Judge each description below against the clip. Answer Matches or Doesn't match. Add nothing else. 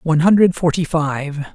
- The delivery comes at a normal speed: Matches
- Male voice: Matches